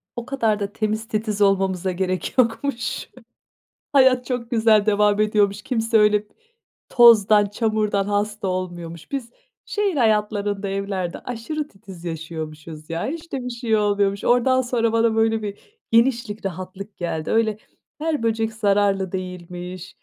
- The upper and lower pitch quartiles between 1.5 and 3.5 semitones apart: Yes, average, 3.0 semitones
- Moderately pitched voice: No, high, 210 Hz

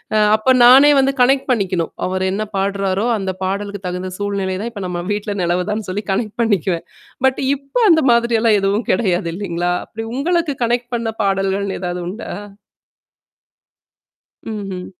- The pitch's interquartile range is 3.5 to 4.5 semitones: Yes, average, 3.9 semitones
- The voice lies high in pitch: Yes, high, 200 Hz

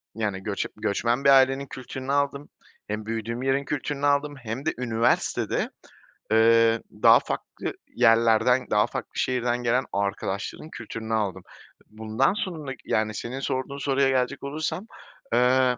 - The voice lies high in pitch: No, low, 125 Hz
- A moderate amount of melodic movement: Yes, average, 3.6 semitones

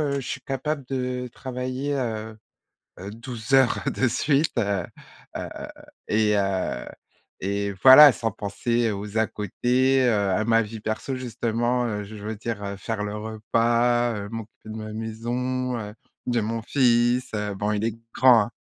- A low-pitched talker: Yes, low, 115 Hz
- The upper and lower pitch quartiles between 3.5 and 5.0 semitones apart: No, average, 3.1 semitones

